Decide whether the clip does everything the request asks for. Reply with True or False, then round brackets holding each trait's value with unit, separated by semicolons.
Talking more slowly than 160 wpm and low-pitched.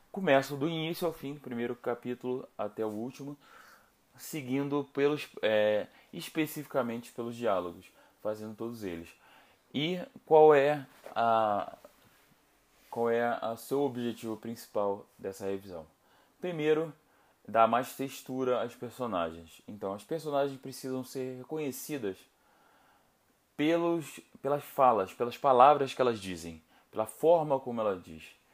True (120 wpm; 125 Hz)